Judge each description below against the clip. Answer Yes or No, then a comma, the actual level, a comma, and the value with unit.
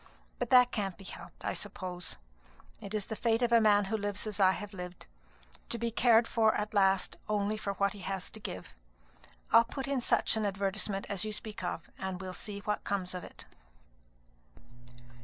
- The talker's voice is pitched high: Yes, high, 205 Hz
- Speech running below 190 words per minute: No, average, 195 wpm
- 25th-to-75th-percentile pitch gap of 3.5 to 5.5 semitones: No, narrow, 2.5 semitones